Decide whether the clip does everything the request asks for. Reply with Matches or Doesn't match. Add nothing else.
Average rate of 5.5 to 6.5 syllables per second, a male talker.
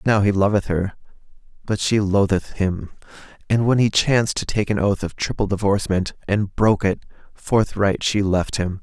Doesn't match